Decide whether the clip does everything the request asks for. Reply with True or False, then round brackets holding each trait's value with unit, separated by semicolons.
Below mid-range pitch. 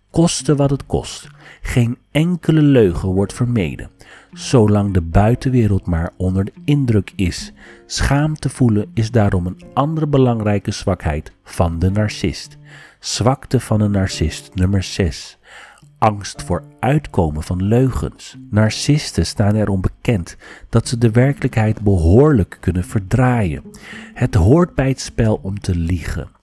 True (110 Hz)